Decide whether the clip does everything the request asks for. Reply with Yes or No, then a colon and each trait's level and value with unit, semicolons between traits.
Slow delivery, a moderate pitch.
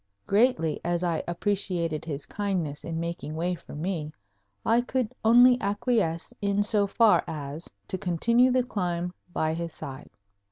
No: average, 150 wpm; medium, 180 Hz